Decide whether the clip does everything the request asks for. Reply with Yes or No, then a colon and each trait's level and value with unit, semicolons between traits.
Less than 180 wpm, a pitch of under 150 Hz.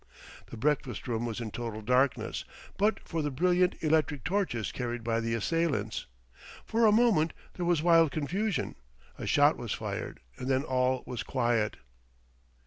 Yes: average, 155 wpm; low, 135 Hz